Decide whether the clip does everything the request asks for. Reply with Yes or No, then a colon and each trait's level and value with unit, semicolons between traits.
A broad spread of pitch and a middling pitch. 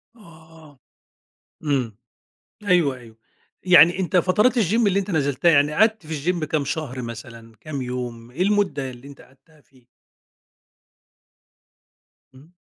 Yes: wide, 5.7 semitones; medium, 150 Hz